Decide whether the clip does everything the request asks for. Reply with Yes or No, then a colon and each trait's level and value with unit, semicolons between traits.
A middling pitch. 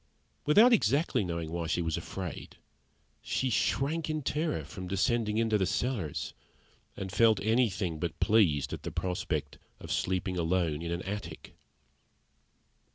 No: very low, 95 Hz